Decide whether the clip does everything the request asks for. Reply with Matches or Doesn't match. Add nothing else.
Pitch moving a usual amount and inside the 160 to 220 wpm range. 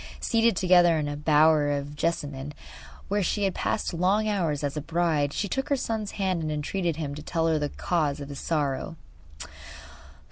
Matches